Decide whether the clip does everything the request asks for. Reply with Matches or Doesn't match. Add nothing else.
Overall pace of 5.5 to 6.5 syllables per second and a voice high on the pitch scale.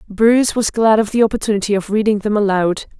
Matches